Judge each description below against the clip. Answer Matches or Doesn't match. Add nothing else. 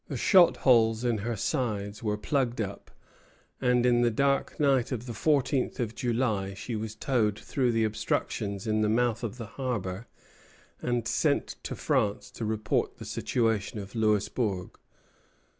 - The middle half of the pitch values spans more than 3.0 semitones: Doesn't match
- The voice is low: Matches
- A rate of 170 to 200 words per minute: Doesn't match